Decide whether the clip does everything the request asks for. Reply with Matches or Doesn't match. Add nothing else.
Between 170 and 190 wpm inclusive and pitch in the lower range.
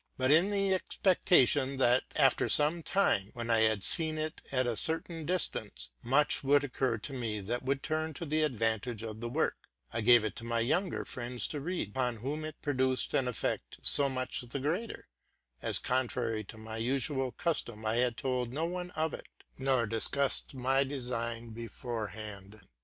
Matches